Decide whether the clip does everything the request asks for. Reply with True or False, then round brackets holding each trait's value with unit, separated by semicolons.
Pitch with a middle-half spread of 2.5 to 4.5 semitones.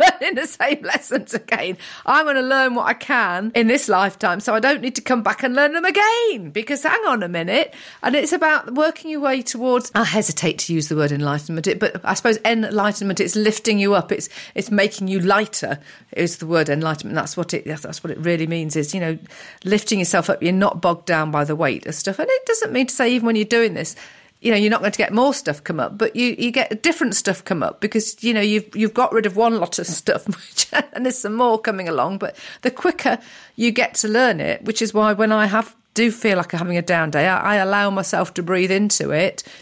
False (5.1 semitones)